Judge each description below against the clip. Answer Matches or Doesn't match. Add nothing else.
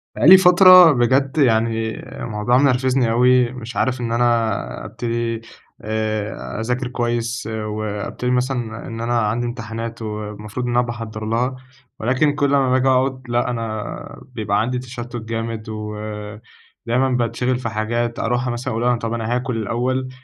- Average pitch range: Doesn't match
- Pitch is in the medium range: Doesn't match